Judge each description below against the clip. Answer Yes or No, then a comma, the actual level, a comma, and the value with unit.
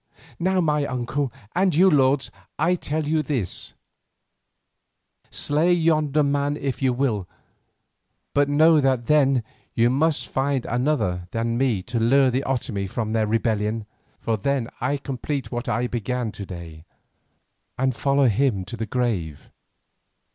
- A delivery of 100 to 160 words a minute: Yes, average, 140 wpm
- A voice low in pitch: Yes, low, 130 Hz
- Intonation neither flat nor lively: Yes, average, 4.1 semitones